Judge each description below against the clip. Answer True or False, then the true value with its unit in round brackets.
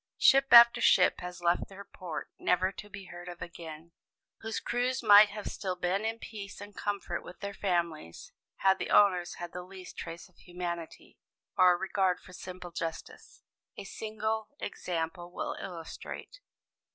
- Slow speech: False (160 wpm)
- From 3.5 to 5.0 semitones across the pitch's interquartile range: False (2.8 semitones)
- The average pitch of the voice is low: False (185 Hz)